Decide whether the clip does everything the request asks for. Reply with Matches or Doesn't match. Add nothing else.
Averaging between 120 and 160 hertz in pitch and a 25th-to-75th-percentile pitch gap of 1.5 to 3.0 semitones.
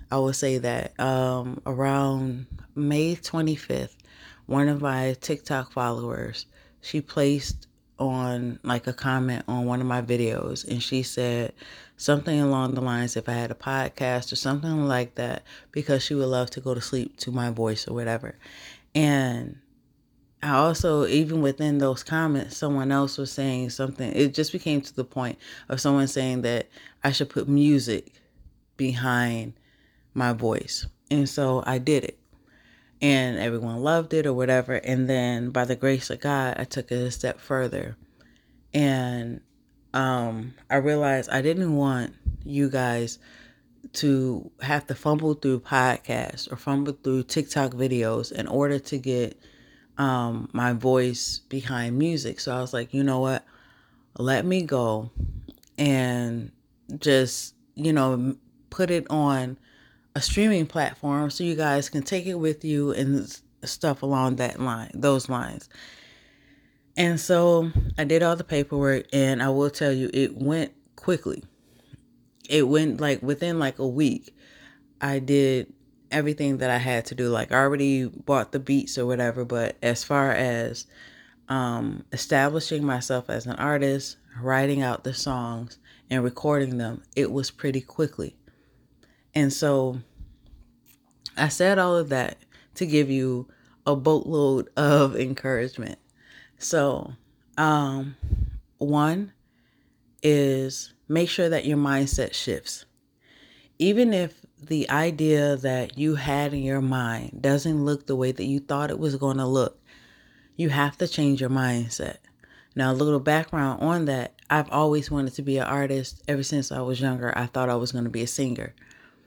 Matches